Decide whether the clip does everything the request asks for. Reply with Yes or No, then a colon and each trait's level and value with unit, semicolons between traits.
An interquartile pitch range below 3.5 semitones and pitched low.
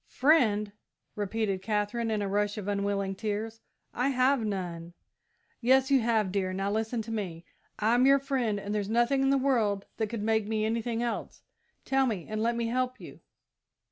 No: average, 2.9 semitones; high, 220 Hz